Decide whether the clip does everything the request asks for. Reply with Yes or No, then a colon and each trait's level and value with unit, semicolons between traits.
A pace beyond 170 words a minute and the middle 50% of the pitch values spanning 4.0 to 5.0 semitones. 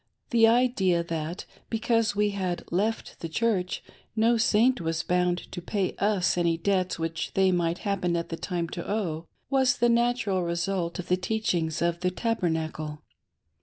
No: average, 165 wpm; average, 4.4 semitones